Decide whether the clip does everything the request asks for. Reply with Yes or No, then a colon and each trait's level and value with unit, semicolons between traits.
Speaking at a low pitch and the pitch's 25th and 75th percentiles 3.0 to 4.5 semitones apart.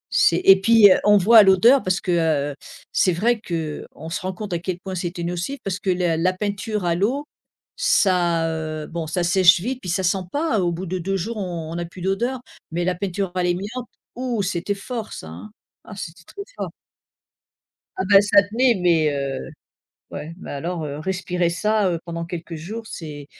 No: medium, 180 Hz; average, 3.4 semitones